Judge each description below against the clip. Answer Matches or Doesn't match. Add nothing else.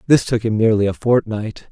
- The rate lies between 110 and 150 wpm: Doesn't match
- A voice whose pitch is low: Matches